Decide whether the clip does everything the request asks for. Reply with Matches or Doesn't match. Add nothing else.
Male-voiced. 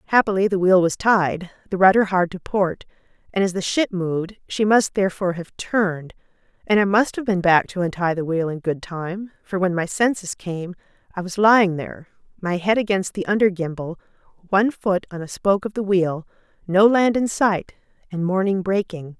Doesn't match